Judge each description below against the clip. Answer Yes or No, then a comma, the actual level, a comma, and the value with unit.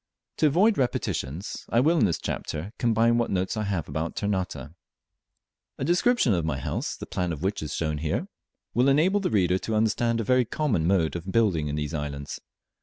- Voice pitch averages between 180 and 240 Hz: No, low, 100 Hz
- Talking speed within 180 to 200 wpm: Yes, average, 195 wpm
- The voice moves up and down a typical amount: No, wide, 7.0 semitones